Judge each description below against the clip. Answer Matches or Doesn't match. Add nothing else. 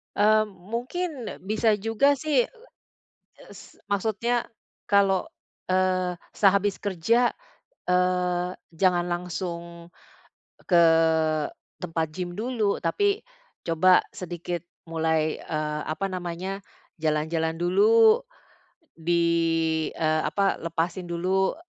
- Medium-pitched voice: Matches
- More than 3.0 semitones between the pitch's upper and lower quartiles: Matches